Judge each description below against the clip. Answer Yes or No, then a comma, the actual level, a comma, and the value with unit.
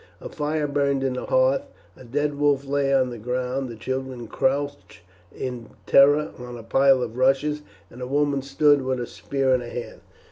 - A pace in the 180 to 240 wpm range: Yes, average, 190 wpm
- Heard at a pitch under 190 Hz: Yes, low, 135 Hz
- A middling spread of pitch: No, narrow, 2.1 semitones